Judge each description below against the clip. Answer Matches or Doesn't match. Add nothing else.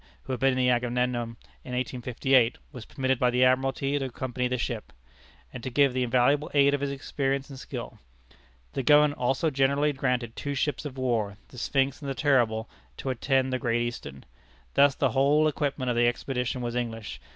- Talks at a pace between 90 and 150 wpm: Doesn't match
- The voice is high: Doesn't match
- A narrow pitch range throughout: Matches